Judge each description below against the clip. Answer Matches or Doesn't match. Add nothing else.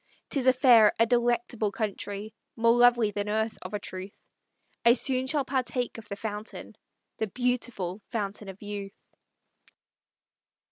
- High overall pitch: Matches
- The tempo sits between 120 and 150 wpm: Matches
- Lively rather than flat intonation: Doesn't match